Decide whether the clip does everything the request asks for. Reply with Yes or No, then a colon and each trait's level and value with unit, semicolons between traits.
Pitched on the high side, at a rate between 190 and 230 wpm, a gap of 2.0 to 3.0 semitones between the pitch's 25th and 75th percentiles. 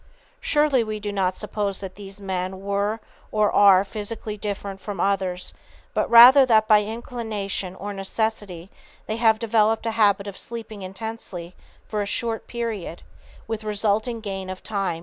No: high, 205 Hz; average, 165 wpm; narrow, 2.4 semitones